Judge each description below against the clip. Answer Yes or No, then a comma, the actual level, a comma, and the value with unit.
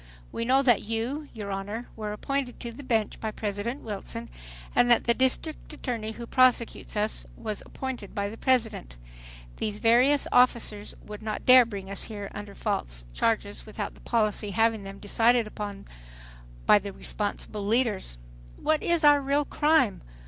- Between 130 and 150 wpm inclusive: No, average, 165 wpm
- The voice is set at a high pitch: Yes, high, 225 Hz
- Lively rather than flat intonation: No, average, 3.6 semitones